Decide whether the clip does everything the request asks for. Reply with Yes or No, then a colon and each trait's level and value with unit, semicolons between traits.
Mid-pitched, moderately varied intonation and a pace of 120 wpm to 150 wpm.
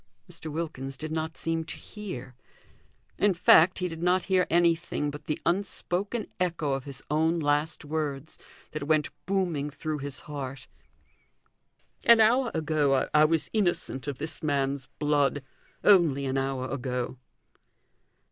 Yes: medium, 155 Hz; average, 3.6 semitones; average, 140 wpm